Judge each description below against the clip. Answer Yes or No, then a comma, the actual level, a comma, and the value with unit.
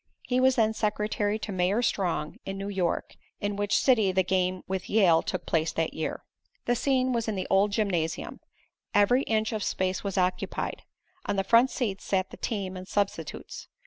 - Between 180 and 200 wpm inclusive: Yes, average, 185 wpm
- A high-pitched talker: Yes, high, 200 Hz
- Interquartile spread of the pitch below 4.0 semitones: Yes, average, 2.9 semitones